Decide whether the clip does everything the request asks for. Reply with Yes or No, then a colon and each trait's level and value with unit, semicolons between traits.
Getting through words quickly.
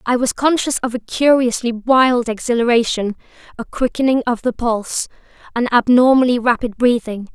No: average, 140 wpm